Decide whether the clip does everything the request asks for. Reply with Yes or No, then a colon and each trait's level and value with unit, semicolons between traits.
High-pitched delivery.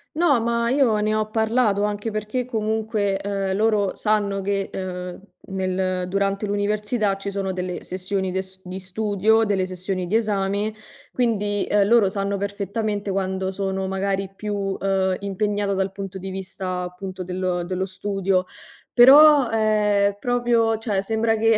Yes: high, 200 Hz